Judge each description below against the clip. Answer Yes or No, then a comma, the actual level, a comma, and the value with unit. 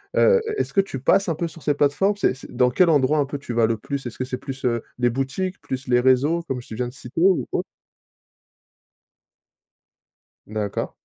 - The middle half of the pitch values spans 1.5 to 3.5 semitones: No, average, 4.7 semitones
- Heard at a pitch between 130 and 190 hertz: Yes, low, 135 Hz